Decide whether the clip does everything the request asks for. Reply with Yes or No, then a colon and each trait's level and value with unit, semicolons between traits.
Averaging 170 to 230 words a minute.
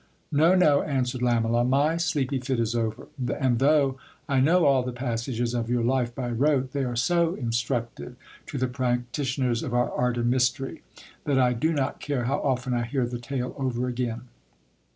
Yes: average, 185 wpm